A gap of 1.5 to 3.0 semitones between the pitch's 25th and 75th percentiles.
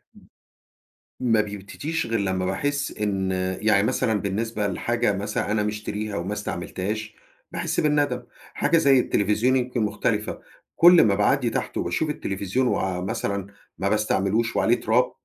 No: average, 3.6 semitones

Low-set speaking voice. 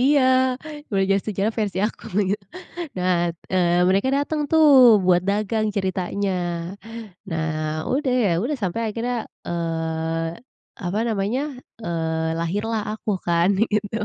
No: high, 195 Hz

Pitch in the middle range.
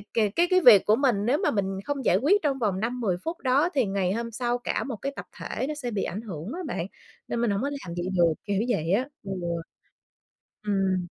No: high, 225 Hz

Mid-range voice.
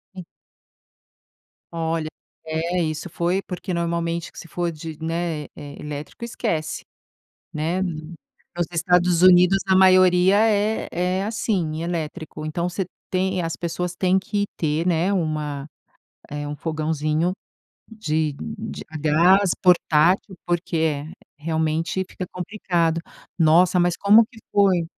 Yes: medium, 170 Hz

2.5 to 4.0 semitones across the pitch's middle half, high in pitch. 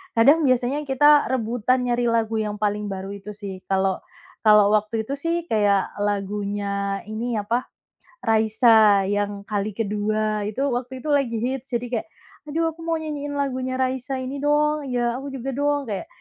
No: average, 4.4 semitones; high, 235 Hz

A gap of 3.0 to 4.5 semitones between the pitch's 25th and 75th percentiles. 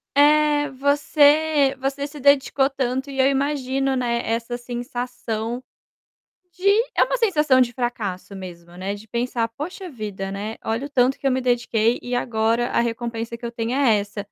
Yes: average, 3.5 semitones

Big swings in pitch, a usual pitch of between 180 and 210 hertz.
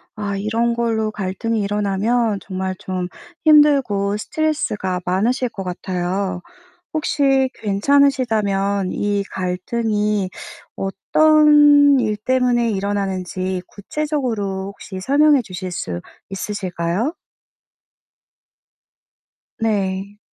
No: average, 4.7 semitones; high, 205 Hz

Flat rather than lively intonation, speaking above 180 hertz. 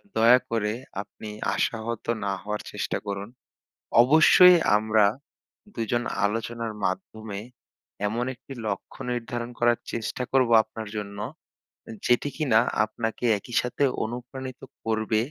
No: narrow, 2.2 semitones; low, 115 Hz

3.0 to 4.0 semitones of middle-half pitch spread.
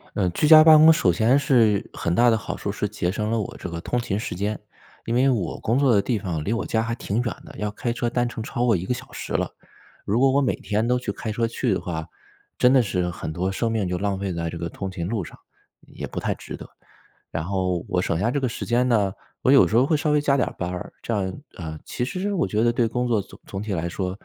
No: average, 4.8 semitones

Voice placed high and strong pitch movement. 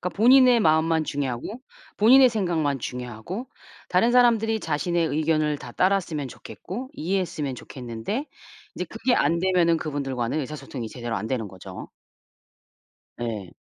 No: medium, 160 Hz; wide, 7.7 semitones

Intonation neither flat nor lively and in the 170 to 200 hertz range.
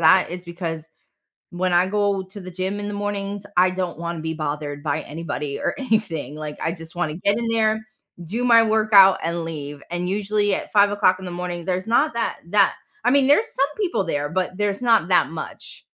Yes: average, 3.8 semitones; medium, 185 Hz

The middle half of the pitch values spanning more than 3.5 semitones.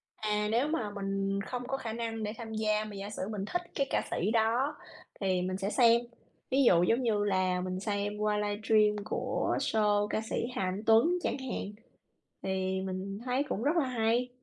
No: average, 2.9 semitones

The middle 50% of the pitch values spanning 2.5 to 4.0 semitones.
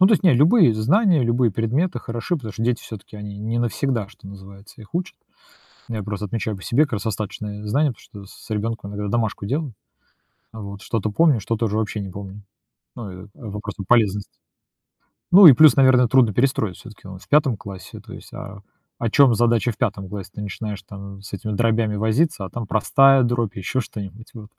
Yes: average, 3.2 semitones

